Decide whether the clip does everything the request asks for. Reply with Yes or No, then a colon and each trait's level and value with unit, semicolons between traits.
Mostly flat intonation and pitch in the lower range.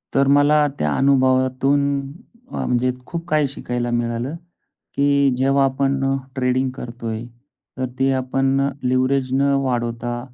Yes: narrow, 1.7 semitones; low, 130 Hz